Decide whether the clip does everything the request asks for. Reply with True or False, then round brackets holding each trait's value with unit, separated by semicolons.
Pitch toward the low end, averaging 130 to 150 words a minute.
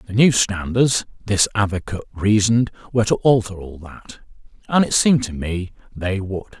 False (105 Hz; 165 wpm)